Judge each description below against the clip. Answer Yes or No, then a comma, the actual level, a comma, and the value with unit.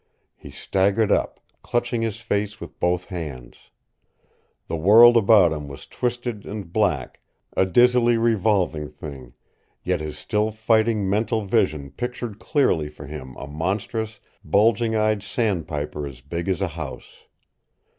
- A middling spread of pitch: No, wide, 6.3 semitones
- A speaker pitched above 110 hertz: No, low, 100 Hz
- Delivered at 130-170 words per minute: Yes, slow, 135 wpm